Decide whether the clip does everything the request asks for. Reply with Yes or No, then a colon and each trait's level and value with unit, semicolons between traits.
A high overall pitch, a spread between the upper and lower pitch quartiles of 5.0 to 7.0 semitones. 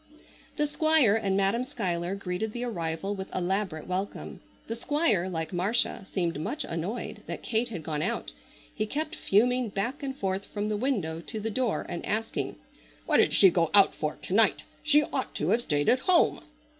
Yes: high, 205 Hz; wide, 5.4 semitones